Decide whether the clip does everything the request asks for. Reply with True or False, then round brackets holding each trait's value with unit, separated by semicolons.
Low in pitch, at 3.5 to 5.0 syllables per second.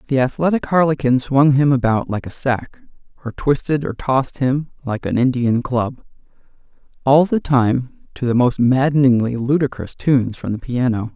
True (130 Hz; 4.9 syllables/s)